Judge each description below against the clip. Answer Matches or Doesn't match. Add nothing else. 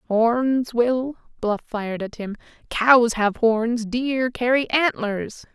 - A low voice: Doesn't match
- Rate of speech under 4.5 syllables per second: Matches